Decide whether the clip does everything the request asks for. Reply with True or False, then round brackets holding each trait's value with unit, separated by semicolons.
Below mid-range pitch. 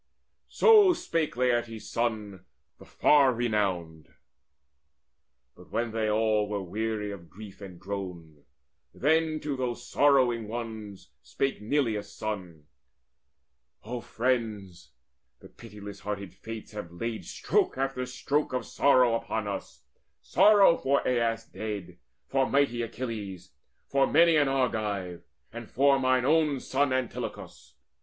True (115 Hz)